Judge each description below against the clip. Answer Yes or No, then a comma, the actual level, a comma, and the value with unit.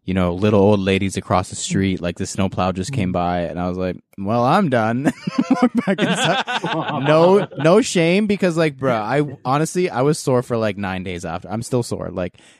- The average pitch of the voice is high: No, low, 110 Hz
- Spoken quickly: No, average, 195 wpm